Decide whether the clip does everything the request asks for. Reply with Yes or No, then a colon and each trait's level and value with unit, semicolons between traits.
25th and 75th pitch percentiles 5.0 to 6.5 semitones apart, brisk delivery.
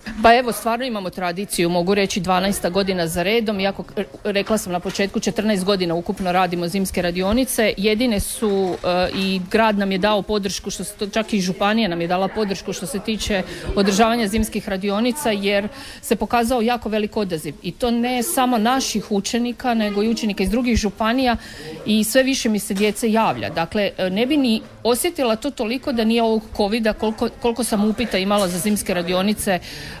No: average, 2.9 semitones; fast, 180 wpm